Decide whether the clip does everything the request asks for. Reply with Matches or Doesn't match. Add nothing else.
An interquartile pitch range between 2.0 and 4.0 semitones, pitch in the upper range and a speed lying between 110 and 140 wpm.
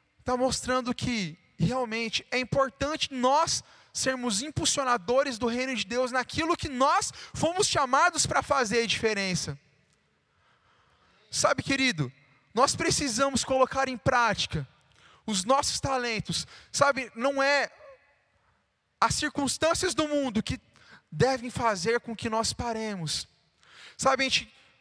Matches